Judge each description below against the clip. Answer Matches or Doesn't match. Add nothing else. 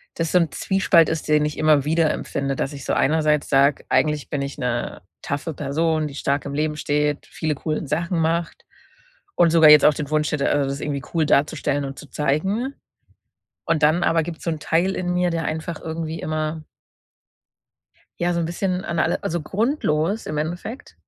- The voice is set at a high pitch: Doesn't match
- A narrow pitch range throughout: Matches